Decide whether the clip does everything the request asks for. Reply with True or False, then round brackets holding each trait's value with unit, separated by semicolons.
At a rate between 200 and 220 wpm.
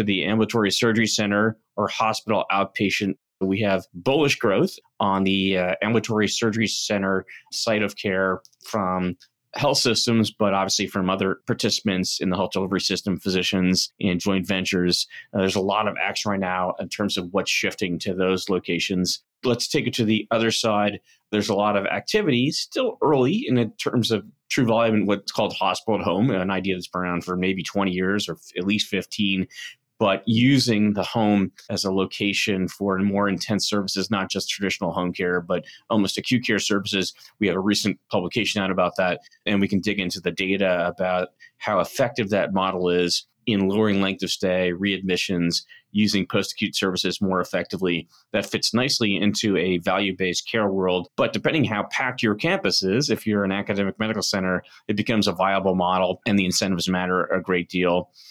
False (185 wpm)